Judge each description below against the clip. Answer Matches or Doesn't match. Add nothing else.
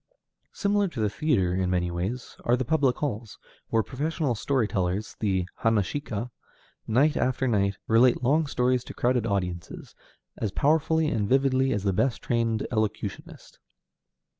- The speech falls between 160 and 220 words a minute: Doesn't match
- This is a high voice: Doesn't match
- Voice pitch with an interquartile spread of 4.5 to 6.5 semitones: Matches